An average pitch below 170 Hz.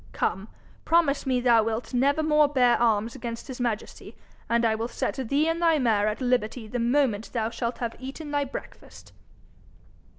No: high, 245 Hz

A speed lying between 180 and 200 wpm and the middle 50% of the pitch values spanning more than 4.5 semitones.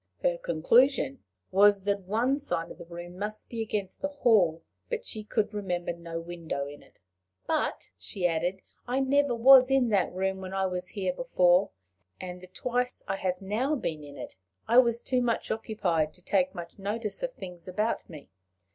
Yes: average, 185 wpm; average, 5.1 semitones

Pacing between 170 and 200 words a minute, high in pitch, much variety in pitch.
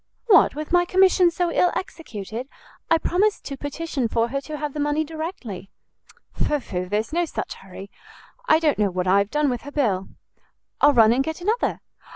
Yes: average, 195 wpm; very high, 290 Hz; wide, 7.0 semitones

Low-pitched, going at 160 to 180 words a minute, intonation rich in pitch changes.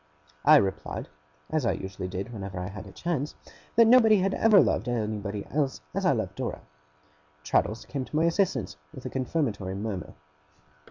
Yes: low, 120 Hz; average, 170 wpm; wide, 8.1 semitones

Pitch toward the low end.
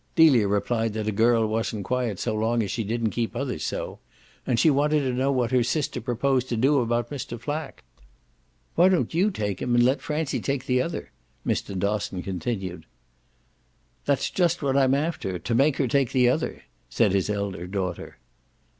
Yes: low, 120 Hz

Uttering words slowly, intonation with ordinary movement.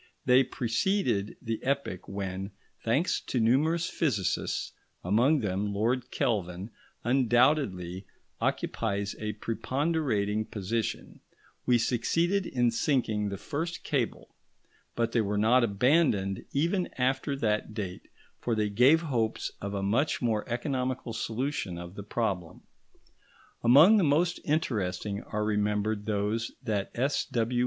Yes: slow, 120 wpm; average, 4.7 semitones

